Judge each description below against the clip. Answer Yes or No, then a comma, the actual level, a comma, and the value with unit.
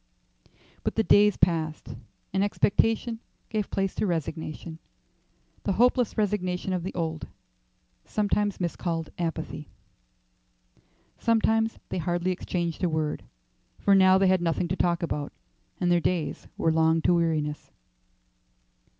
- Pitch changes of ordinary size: Yes, average, 3.6 semitones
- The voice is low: No, medium, 175 Hz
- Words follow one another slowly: Yes, slow, 125 wpm